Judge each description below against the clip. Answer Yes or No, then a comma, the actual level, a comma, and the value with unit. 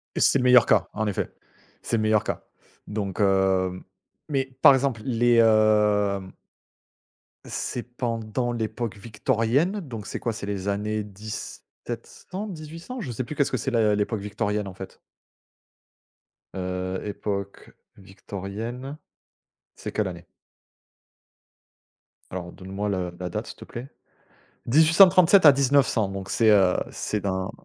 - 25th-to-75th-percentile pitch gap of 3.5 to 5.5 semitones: Yes, average, 4.2 semitones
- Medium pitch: No, low, 110 Hz